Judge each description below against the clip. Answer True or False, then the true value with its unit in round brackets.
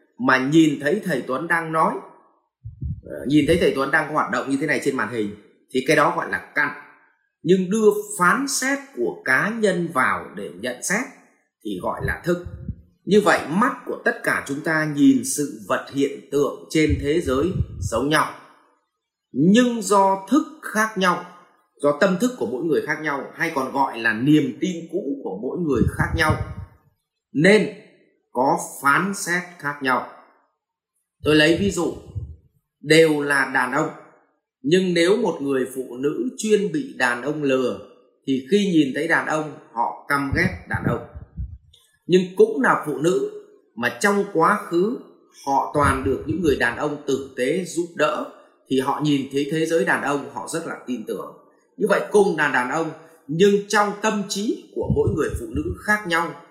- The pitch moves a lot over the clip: True (5.9 semitones)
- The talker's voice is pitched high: False (160 Hz)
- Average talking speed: True (180 wpm)